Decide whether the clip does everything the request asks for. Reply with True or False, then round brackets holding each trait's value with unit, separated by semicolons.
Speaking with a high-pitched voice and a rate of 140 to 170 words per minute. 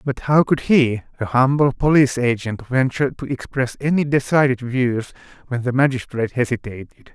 False (130 Hz; 150 wpm)